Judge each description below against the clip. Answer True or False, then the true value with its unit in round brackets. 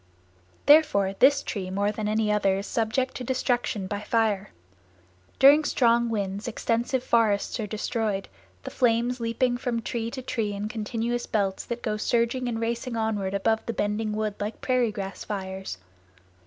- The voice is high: True (225 Hz)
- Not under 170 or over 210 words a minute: False (160 wpm)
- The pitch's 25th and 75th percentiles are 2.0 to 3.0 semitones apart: True (2.7 semitones)